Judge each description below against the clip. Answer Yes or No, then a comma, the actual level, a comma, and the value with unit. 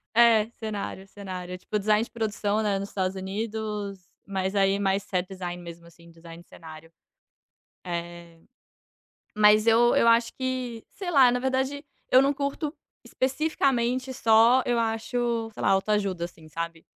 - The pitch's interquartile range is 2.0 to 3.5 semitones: No, average, 4.3 semitones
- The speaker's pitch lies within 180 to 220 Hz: Yes, high, 210 Hz